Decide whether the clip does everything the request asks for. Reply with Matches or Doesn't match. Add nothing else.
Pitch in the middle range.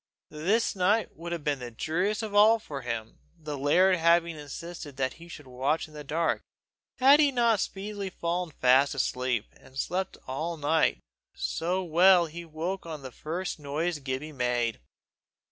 Matches